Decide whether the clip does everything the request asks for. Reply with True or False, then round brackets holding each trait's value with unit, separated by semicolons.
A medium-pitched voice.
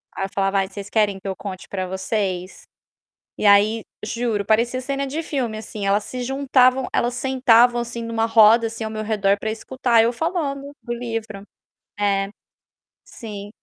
False (225 Hz)